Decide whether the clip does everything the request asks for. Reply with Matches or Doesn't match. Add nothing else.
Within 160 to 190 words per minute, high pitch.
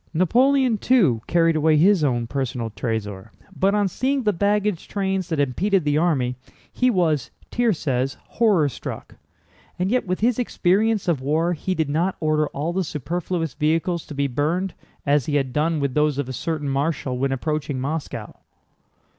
Doesn't match